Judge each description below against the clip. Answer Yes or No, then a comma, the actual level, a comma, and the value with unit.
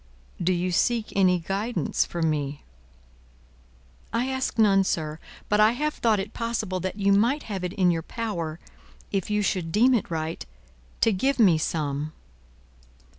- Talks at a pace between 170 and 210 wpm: No, average, 160 wpm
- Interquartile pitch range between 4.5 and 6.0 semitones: Yes, average, 5.0 semitones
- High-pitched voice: Yes, high, 195 Hz